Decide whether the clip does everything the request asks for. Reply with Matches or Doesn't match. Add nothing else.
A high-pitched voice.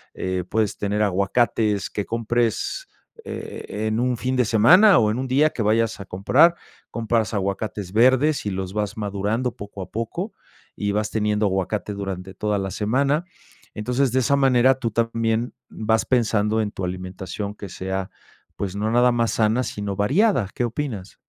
Doesn't match